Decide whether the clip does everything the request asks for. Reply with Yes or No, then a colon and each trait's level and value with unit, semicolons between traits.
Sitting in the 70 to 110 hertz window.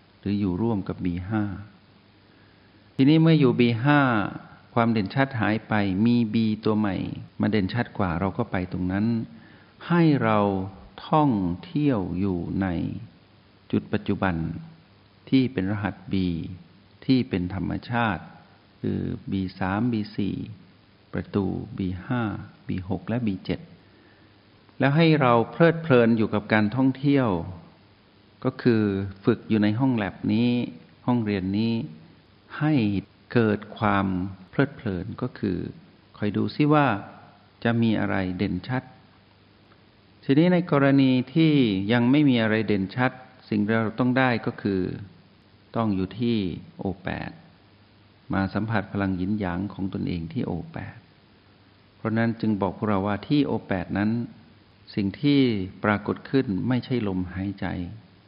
Yes: low, 105 Hz